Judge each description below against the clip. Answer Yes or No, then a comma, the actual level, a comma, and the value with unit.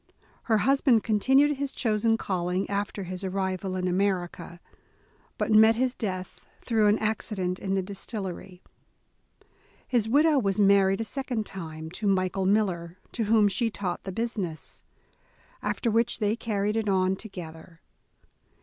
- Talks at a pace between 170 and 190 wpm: No, average, 145 wpm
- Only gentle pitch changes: No, average, 3.3 semitones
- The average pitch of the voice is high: Yes, high, 200 Hz